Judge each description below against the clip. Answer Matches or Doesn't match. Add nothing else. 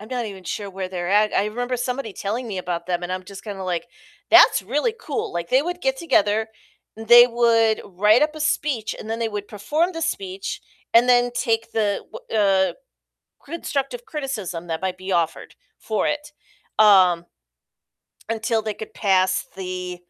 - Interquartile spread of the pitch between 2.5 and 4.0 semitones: Doesn't match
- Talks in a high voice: Matches